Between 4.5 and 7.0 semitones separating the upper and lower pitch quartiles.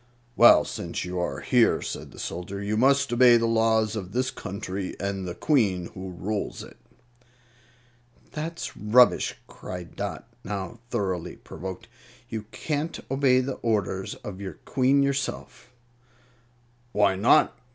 Yes: average, 5.1 semitones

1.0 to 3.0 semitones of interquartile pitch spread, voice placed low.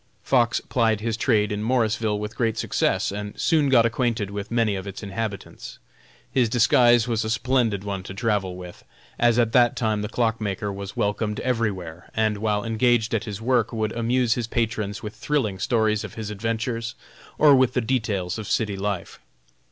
Yes: narrow, 2.4 semitones; low, 110 Hz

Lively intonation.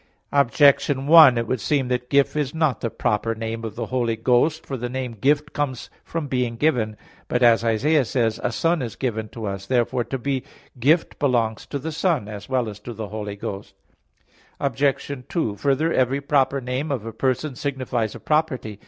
No: average, 3.9 semitones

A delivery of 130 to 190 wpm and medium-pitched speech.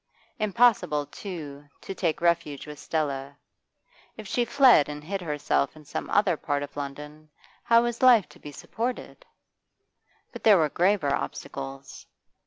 Yes: average, 145 wpm; medium, 155 Hz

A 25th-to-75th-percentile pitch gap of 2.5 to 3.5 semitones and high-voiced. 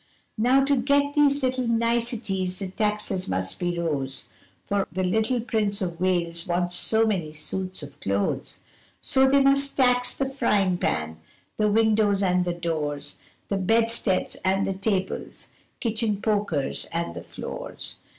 No: average, 4.9 semitones; high, 200 Hz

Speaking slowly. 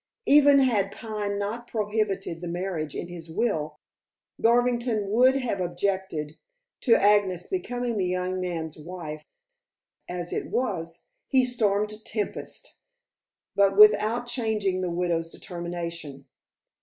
Yes: slow, 120 wpm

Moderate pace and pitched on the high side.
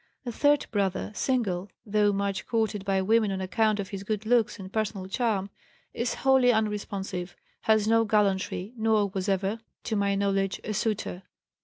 Yes: average, 165 wpm; high, 205 Hz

